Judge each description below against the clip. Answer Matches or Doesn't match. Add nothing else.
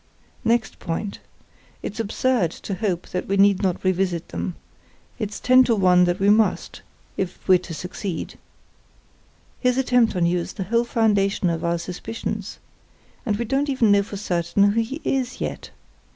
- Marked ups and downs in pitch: Doesn't match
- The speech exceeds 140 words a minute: Matches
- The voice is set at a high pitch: Matches